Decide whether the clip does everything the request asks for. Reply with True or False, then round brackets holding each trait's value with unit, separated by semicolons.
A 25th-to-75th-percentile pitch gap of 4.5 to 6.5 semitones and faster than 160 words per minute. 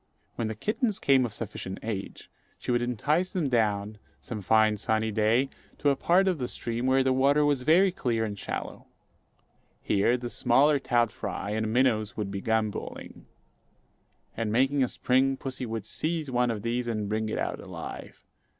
False (3.7 semitones; 175 wpm)